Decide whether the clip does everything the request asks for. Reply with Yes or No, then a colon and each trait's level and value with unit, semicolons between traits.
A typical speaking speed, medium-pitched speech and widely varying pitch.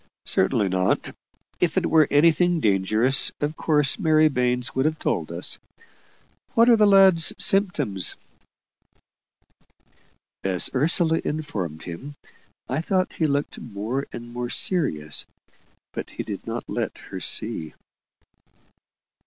No: slow, 120 wpm; medium, 145 Hz; wide, 6.9 semitones